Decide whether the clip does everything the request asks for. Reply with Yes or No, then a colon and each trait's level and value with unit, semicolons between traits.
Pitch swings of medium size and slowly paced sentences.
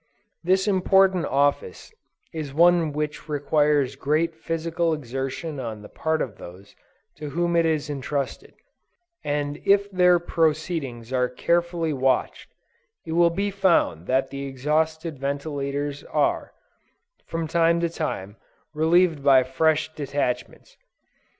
Yes: average, 3.5 semitones; slow, 125 wpm